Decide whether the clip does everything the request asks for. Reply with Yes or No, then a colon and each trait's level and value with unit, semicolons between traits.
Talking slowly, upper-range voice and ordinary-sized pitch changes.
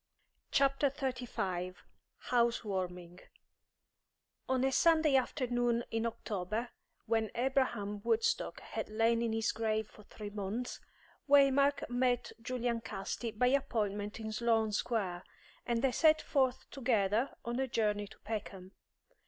Yes: slow, 125 wpm; high, 230 Hz; average, 3.5 semitones